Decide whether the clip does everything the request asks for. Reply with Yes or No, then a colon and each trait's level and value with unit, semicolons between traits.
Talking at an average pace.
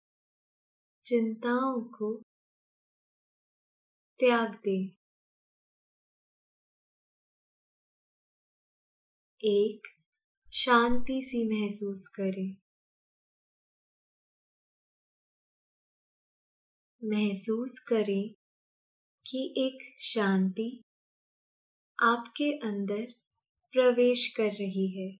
No: slow, 45 wpm